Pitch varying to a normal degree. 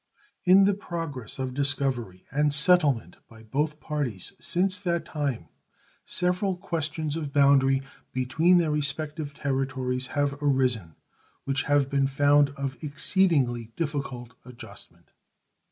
Yes: average, 3.2 semitones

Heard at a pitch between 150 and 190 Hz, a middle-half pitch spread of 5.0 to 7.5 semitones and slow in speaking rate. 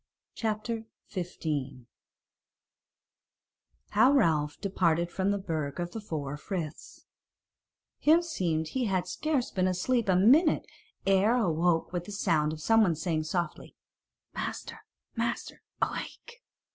Yes: medium, 185 Hz; wide, 5.6 semitones; slow, 115 wpm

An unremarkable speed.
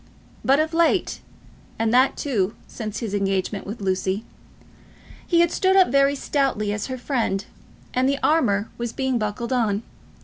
Yes: average, 160 wpm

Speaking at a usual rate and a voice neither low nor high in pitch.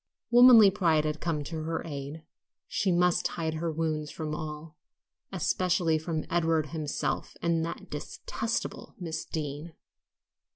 No: slow, 130 wpm; medium, 160 Hz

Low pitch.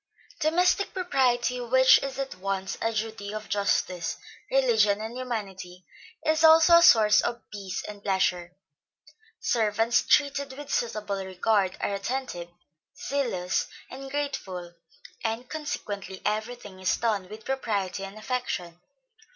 No: high, 220 Hz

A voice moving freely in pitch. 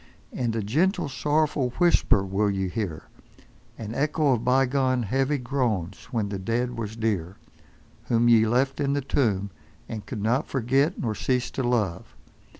No: average, 4.1 semitones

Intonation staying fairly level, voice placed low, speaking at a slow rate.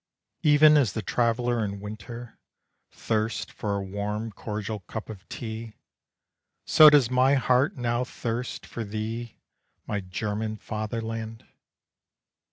Yes: narrow, 2.3 semitones; low, 110 Hz; slow, 120 wpm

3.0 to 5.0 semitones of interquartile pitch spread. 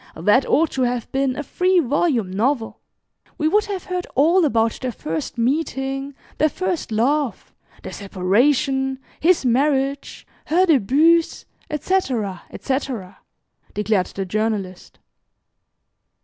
No: wide, 5.5 semitones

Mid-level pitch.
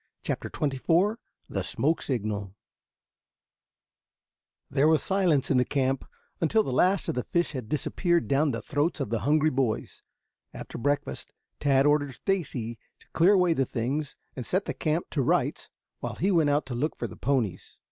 Yes: medium, 145 Hz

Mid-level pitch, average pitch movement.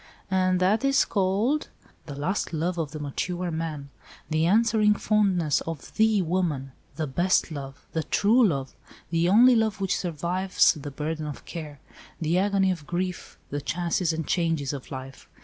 Yes: medium, 175 Hz; average, 4.2 semitones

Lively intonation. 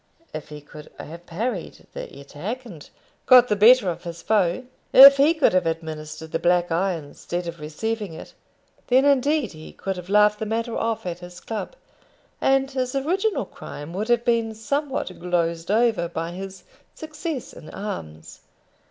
Yes: wide, 6.6 semitones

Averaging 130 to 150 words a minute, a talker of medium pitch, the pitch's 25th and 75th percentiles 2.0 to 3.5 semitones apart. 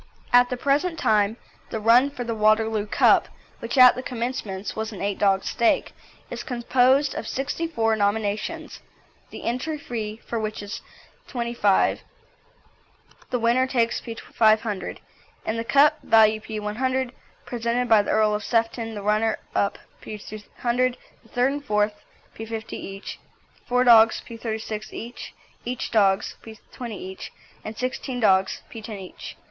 No: average, 140 wpm; high, 225 Hz; narrow, 2.6 semitones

